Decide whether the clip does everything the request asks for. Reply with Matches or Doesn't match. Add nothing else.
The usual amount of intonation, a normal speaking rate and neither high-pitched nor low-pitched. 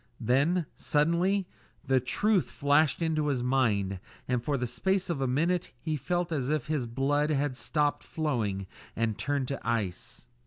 Matches